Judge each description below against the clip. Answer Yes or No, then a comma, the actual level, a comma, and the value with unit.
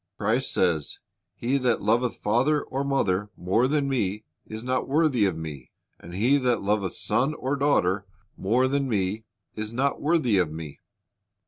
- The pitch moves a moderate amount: No, wide, 5.7 semitones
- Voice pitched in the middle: No, low, 115 Hz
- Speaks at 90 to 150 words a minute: No, average, 160 wpm